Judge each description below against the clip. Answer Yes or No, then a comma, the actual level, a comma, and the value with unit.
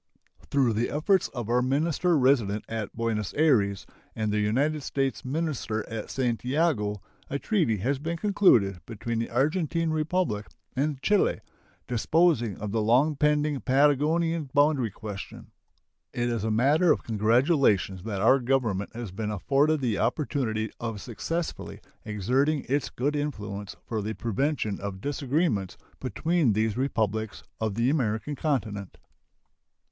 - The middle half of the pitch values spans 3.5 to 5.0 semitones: No, wide, 5.5 semitones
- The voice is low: Yes, low, 125 Hz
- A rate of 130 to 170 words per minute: Yes, slow, 135 wpm